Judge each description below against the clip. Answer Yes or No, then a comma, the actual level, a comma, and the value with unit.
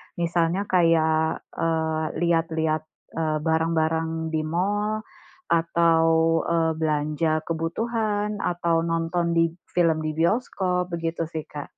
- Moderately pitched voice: Yes, medium, 165 Hz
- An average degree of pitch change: No, narrow, 1.3 semitones